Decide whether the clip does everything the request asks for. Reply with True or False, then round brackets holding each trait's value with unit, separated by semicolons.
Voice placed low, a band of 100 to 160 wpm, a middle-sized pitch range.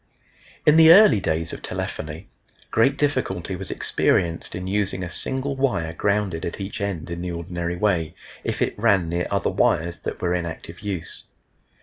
False (90 Hz; 175 wpm; 3.8 semitones)